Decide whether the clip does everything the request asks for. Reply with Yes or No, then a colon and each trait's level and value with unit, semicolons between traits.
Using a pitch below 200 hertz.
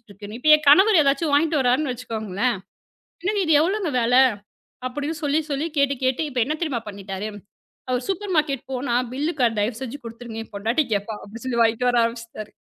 No: very high, 255 Hz